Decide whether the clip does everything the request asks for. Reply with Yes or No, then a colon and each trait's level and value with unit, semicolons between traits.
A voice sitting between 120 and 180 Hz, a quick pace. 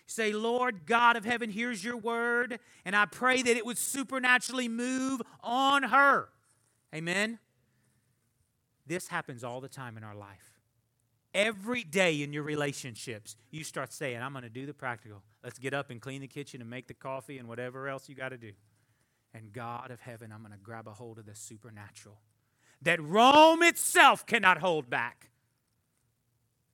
No: low, 135 Hz; average, 175 wpm